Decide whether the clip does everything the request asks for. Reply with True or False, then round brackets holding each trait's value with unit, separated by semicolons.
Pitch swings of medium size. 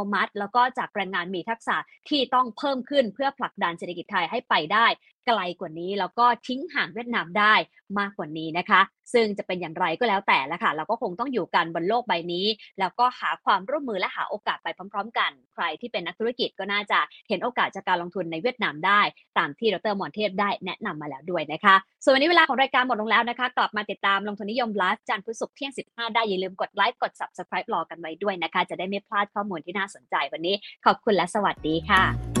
True (4.5 semitones)